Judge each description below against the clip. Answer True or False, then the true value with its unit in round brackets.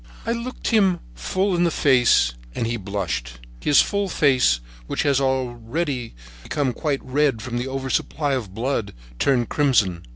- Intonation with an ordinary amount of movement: True (4.6 semitones)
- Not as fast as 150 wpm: True (140 wpm)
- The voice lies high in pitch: False (130 Hz)